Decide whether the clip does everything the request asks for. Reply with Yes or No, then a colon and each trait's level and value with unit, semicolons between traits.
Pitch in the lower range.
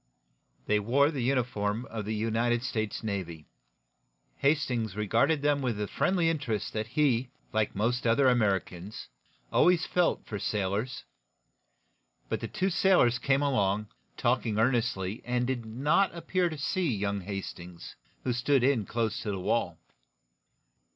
Yes: low, 120 Hz